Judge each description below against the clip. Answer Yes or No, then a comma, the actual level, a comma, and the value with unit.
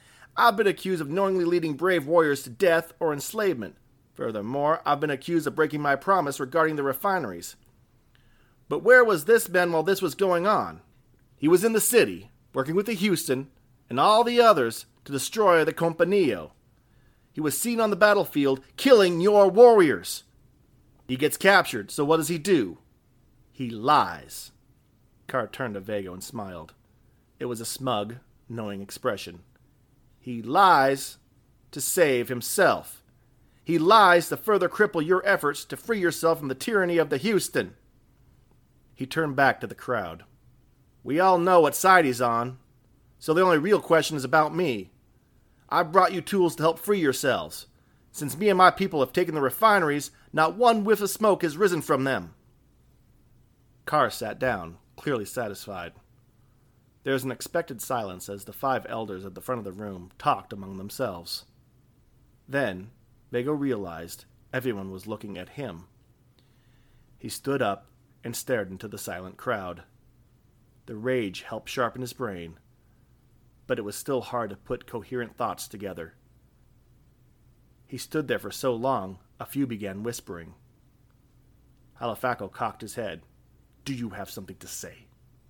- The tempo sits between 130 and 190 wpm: Yes, average, 160 wpm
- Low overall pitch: Yes, low, 130 Hz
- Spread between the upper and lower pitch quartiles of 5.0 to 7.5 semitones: Yes, wide, 5.5 semitones